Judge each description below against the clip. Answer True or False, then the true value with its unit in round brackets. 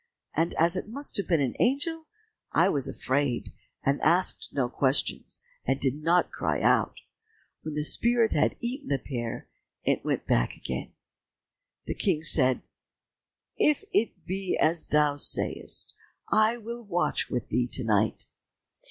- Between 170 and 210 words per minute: False (150 wpm)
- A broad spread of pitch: True (8.3 semitones)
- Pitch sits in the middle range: True (155 Hz)